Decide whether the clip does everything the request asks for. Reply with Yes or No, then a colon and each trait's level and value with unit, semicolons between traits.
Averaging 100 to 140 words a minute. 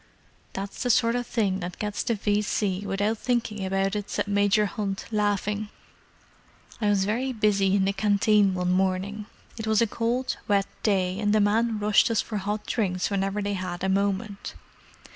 No: average, 165 wpm